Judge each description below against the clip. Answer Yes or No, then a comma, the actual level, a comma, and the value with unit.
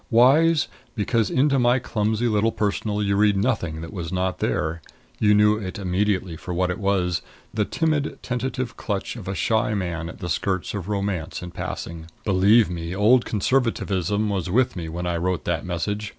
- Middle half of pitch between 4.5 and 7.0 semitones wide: No, average, 3.9 semitones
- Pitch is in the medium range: No, low, 100 Hz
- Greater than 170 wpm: Yes, average, 180 wpm